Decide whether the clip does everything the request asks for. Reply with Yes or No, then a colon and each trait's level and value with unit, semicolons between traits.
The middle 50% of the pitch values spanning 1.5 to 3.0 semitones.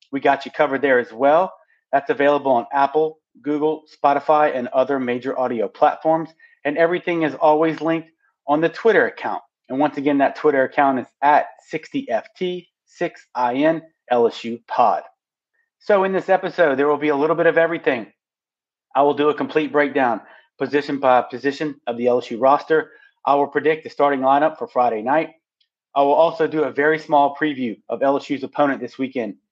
Yes: narrow, 2.6 semitones